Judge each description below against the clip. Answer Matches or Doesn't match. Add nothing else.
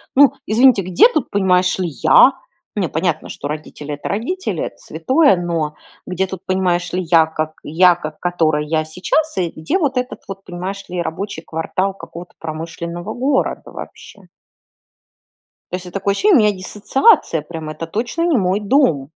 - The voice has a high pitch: Doesn't match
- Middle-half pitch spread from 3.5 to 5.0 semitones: Matches